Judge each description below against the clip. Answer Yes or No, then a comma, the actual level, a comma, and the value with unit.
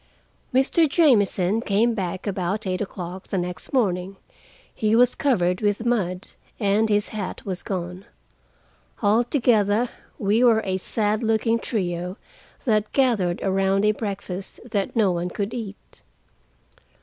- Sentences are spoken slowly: Yes, slow, 130 wpm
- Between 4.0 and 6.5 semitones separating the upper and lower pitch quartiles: No, average, 3.2 semitones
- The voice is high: Yes, high, 205 Hz